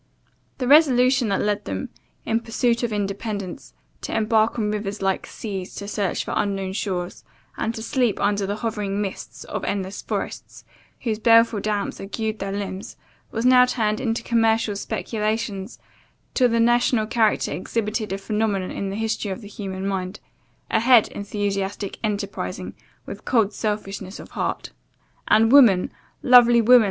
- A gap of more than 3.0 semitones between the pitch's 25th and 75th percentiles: No, narrow, 2.5 semitones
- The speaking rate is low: No, average, 155 wpm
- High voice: Yes, high, 210 Hz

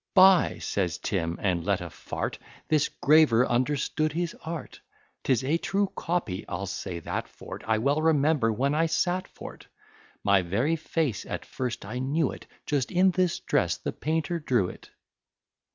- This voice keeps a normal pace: Yes, average, 170 wpm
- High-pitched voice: No, medium, 140 Hz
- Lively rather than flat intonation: Yes, wide, 7.0 semitones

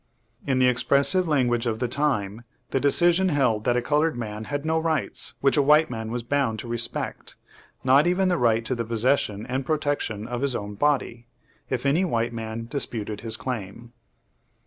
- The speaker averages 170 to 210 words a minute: Yes, average, 185 wpm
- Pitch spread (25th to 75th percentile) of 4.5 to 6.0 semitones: No, average, 4.1 semitones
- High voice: No, low, 125 Hz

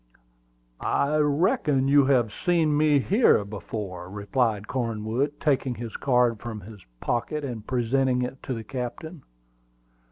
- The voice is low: Yes, low, 125 Hz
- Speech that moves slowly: Yes, slow, 130 wpm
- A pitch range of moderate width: Yes, average, 4.5 semitones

